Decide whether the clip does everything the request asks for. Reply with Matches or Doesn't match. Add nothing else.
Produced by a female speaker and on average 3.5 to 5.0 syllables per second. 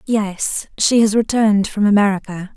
Matches